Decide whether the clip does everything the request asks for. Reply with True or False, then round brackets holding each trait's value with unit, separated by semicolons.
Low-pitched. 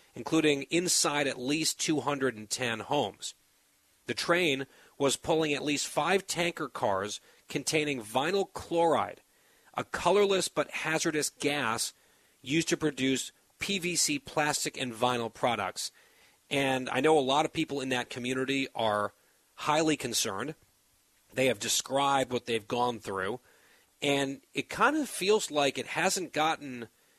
False (145 Hz)